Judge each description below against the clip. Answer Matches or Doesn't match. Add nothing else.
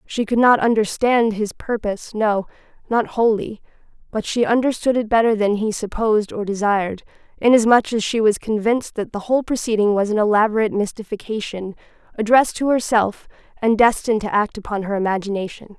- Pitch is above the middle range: Matches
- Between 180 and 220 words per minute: Doesn't match